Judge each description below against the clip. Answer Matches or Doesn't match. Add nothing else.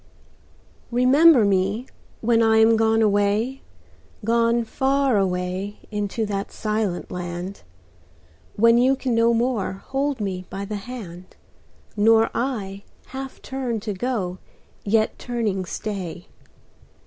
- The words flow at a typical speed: Doesn't match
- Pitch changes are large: Doesn't match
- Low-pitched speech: Doesn't match